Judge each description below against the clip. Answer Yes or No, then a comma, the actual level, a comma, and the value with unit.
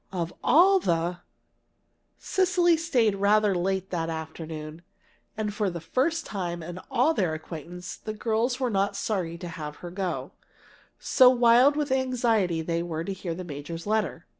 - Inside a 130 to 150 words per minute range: No, average, 165 wpm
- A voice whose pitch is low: No, high, 195 Hz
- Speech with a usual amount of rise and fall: No, wide, 6.4 semitones